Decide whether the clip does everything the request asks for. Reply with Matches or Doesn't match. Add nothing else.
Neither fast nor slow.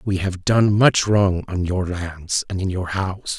Doesn't match